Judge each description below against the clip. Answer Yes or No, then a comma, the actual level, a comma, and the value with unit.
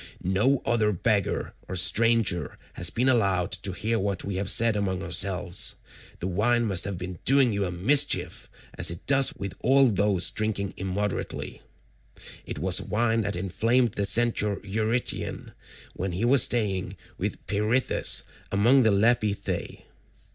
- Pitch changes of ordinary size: Yes, average, 3.5 semitones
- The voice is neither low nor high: No, low, 105 Hz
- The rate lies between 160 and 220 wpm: No, average, 145 wpm